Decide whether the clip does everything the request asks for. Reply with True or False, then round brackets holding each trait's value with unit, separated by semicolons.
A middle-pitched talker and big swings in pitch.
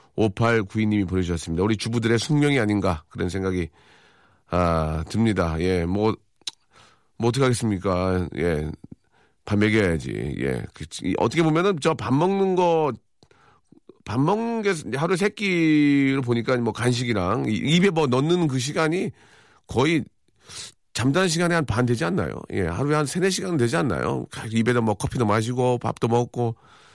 False (120 Hz; 6.7 semitones)